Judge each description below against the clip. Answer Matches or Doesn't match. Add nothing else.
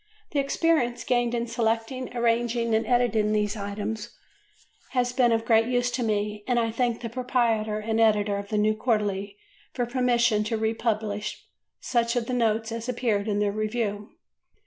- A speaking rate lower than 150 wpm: Doesn't match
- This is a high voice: Matches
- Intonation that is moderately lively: Doesn't match